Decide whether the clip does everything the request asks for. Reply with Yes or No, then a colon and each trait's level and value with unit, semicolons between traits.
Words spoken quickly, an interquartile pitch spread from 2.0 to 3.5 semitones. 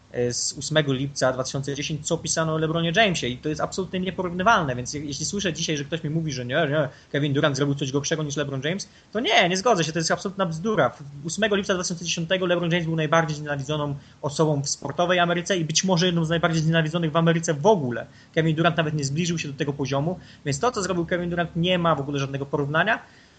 Yes: fast, 220 wpm; average, 3.2 semitones